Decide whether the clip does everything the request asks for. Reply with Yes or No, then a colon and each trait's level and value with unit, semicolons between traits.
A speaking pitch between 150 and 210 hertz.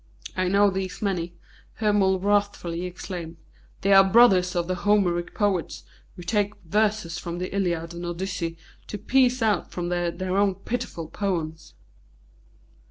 Yes: medium, 185 Hz